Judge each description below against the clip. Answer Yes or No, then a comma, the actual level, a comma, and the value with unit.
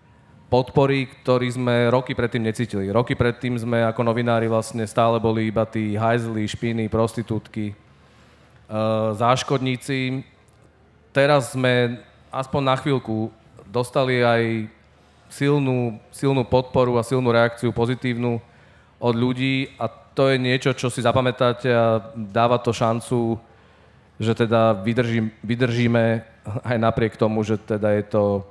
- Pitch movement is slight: Yes, narrow, 2.1 semitones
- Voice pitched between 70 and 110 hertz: No, low, 120 Hz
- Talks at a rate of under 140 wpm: Yes, average, 125 wpm